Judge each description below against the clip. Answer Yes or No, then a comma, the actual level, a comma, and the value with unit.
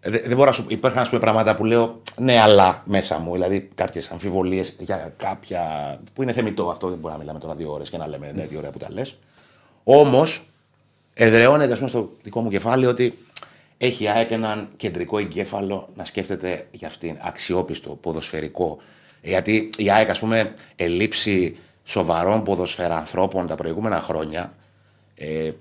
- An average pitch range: Yes, average, 4.5 semitones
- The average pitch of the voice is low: Yes, low, 100 Hz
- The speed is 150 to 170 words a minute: Yes, average, 165 wpm